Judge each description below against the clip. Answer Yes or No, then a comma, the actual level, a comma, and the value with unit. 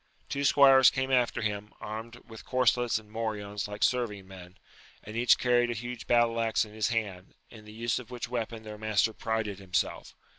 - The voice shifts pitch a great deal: No, narrow, 2.4 semitones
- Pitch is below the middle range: Yes, low, 110 Hz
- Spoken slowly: No, average, 190 wpm